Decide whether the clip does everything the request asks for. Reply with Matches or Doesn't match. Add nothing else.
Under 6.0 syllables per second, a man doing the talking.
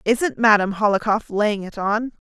Doesn't match